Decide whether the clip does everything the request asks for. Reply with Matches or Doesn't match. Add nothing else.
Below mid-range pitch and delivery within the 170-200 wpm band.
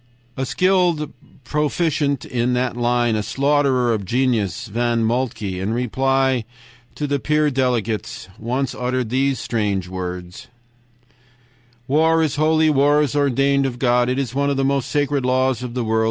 Doesn't match